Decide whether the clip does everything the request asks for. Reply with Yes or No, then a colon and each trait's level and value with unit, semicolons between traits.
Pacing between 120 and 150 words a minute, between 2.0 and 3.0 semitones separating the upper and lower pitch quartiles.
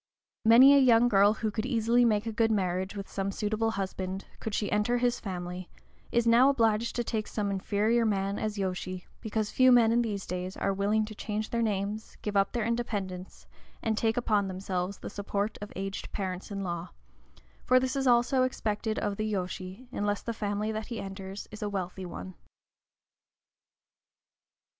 No: average, 180 wpm; average, 2.7 semitones